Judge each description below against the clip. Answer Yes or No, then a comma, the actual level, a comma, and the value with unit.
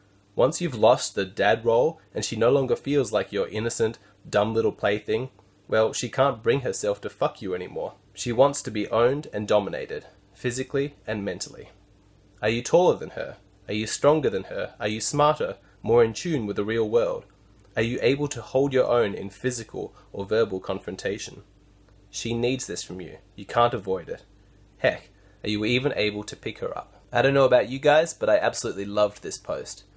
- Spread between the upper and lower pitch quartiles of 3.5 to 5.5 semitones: Yes, average, 4.9 semitones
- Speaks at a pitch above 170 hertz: No, low, 115 Hz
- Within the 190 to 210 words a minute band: Yes, average, 195 wpm